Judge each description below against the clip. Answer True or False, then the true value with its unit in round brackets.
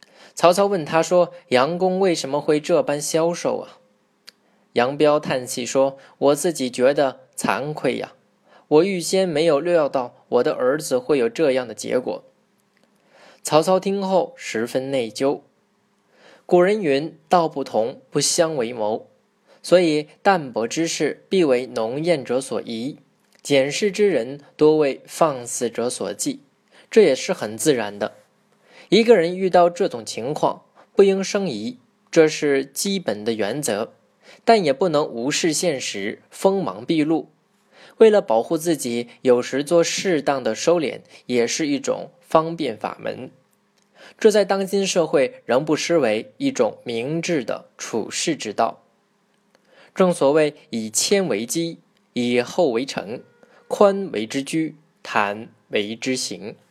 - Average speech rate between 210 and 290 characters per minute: False (200 characters per minute)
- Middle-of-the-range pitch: True (165 Hz)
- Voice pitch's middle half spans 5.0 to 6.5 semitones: True (6.0 semitones)